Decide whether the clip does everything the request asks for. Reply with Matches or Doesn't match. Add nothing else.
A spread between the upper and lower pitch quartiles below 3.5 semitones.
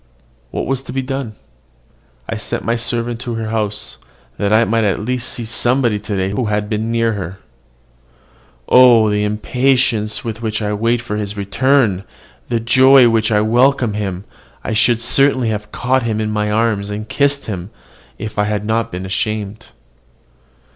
Matches